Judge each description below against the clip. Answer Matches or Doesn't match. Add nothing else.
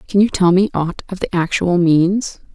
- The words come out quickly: Matches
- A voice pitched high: Doesn't match